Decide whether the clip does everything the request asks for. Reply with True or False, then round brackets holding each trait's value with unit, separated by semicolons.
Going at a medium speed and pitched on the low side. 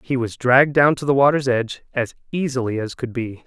False (225 wpm; 130 Hz)